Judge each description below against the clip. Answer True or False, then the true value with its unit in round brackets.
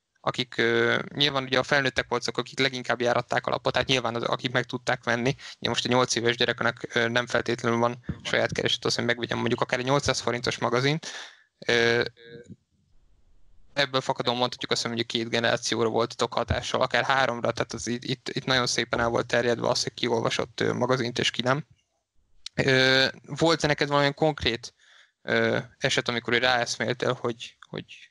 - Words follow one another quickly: True (170 wpm)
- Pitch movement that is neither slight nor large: False (1.9 semitones)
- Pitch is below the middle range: True (120 Hz)